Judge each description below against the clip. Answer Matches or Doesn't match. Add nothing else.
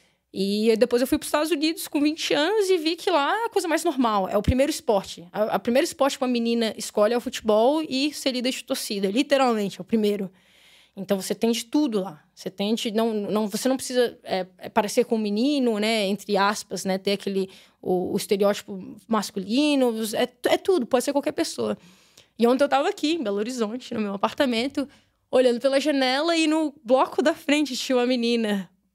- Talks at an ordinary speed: Doesn't match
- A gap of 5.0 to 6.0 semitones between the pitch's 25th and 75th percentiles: Matches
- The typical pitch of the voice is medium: Doesn't match